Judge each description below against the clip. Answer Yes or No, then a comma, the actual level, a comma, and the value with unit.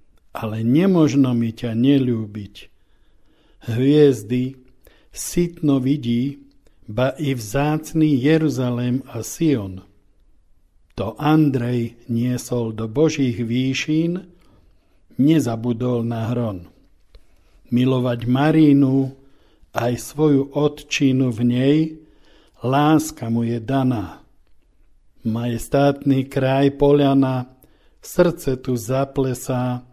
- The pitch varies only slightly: No, average, 3.3 semitones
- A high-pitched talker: No, low, 130 Hz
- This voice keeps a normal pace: No, slow, 80 wpm